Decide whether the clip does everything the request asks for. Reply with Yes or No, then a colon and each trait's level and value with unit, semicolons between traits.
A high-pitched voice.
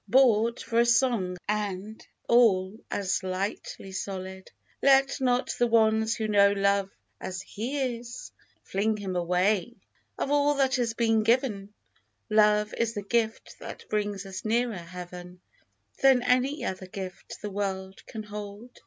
Yes: high, 210 Hz